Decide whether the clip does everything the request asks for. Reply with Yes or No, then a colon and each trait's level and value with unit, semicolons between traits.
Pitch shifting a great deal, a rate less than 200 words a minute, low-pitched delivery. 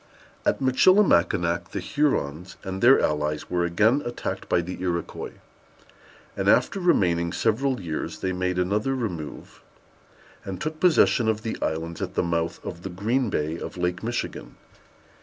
Yes: wide, 5.9 semitones; average, 150 wpm; very low, 95 Hz